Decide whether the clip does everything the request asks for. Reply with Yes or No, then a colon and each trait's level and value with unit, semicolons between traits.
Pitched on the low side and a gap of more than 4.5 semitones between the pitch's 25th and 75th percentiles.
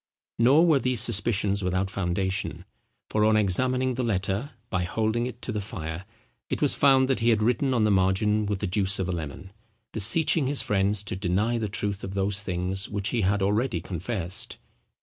No: low, 105 Hz; average, 3.8 semitones